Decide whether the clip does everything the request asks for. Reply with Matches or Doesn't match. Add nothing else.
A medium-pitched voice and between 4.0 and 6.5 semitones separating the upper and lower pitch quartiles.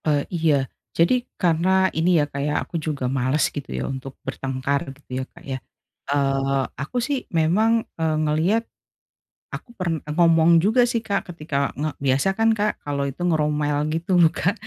Matches